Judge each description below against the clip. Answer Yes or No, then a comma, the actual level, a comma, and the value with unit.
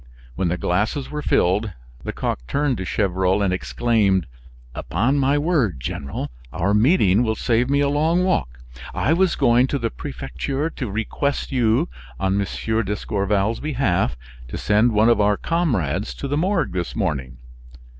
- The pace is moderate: Yes, average, 155 wpm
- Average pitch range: No, wide, 6.8 semitones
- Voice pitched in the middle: No, low, 110 Hz